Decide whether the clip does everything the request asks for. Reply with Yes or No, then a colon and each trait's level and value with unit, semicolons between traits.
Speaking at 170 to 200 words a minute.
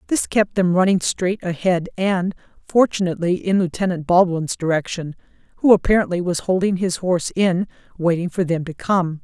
No: average, 155 wpm